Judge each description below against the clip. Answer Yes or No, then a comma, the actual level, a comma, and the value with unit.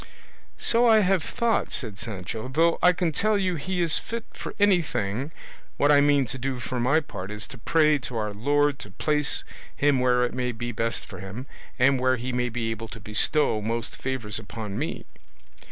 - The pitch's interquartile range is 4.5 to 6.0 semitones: Yes, average, 5.1 semitones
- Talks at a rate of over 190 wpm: Yes, average, 200 wpm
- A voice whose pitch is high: No, low, 130 Hz